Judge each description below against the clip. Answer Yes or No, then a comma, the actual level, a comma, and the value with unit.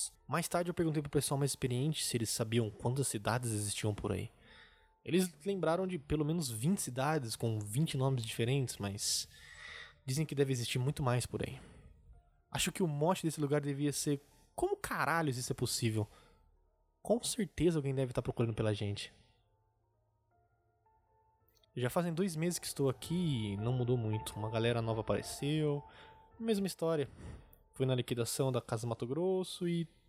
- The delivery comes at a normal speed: Yes, average, 165 wpm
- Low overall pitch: Yes, low, 130 Hz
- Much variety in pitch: Yes, wide, 5.9 semitones